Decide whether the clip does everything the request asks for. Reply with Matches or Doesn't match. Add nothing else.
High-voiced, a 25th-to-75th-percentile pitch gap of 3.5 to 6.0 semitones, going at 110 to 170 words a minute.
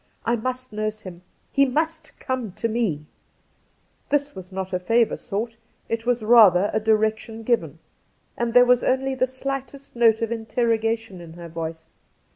Doesn't match